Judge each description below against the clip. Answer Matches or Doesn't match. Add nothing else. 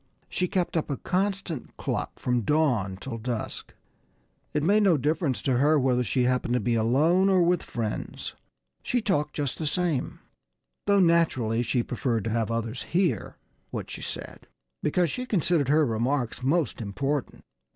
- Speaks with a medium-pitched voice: Matches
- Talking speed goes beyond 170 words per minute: Doesn't match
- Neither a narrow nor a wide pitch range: Doesn't match